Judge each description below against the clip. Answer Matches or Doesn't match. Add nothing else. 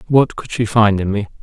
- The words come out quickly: Matches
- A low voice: Matches